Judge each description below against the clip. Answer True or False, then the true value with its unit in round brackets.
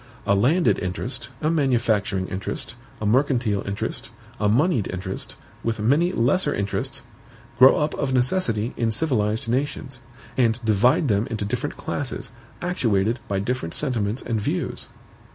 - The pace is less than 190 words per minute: True (135 wpm)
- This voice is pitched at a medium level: False (115 Hz)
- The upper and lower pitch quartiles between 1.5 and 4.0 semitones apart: False (4.5 semitones)